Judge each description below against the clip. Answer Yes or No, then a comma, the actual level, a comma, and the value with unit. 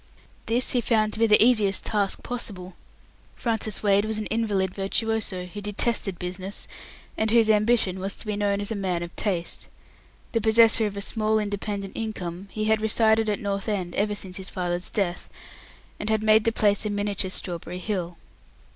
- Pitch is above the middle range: Yes, high, 205 Hz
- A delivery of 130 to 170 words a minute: No, average, 180 wpm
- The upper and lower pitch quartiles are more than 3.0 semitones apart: No, narrow, 2.4 semitones